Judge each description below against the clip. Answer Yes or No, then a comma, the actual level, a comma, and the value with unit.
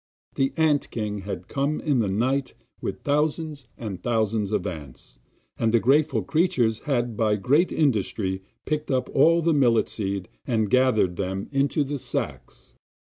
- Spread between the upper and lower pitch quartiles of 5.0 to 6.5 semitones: Yes, wide, 5.5 semitones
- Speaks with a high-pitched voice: No, low, 120 Hz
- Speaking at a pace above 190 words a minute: No, average, 155 wpm